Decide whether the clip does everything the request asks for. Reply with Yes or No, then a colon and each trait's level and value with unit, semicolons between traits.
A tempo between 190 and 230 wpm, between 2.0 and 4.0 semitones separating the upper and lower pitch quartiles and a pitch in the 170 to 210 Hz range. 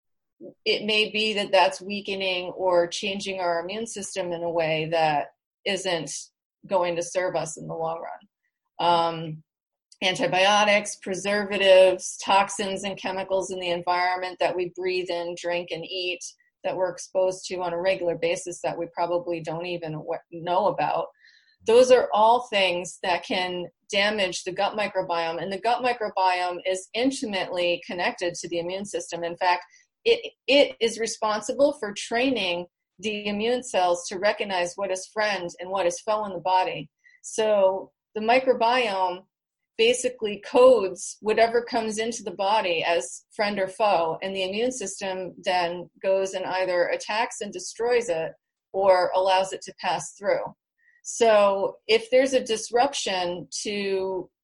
No: average, 150 wpm; average, 3.6 semitones; high, 190 Hz